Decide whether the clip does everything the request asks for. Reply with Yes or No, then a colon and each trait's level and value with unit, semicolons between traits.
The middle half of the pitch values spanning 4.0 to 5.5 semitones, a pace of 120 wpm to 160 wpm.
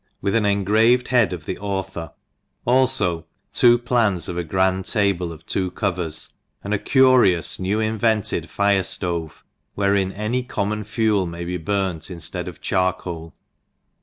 No: average, 3.5 semitones; average, 150 wpm